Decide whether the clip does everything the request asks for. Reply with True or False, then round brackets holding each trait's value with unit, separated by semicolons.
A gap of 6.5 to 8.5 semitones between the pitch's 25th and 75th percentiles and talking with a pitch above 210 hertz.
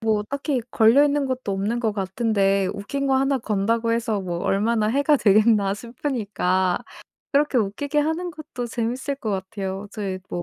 False (5.2 semitones; 225 Hz)